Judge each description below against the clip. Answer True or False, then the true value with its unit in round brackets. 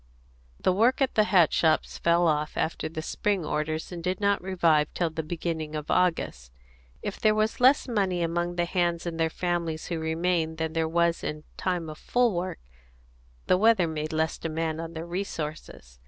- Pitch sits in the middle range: True (170 Hz)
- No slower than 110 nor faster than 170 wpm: False (185 wpm)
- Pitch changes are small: True (2.3 semitones)